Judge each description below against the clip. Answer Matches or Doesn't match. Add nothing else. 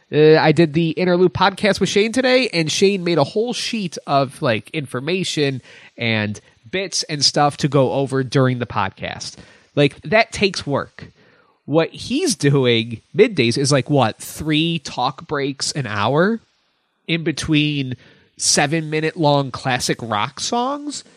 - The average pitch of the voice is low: Doesn't match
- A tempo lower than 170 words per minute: Matches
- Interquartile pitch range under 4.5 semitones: Doesn't match